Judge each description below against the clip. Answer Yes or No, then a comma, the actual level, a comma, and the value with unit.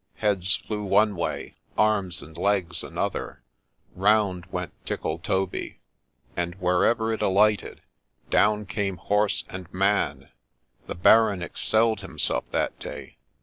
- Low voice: Yes, low, 100 Hz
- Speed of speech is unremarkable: No, slow, 120 wpm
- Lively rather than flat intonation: No, average, 2.8 semitones